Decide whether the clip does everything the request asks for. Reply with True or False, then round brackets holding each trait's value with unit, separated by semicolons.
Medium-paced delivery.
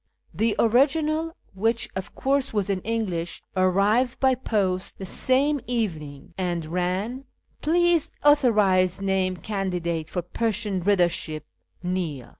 False (125 wpm)